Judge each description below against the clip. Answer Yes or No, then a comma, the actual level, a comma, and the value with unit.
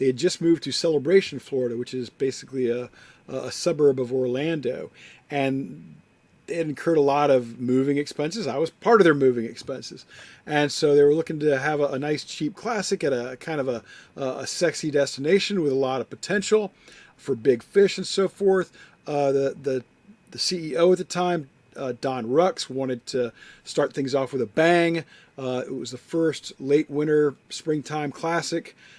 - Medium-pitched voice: Yes, medium, 145 Hz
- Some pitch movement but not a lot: Yes, average, 4.1 semitones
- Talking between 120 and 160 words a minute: No, average, 185 wpm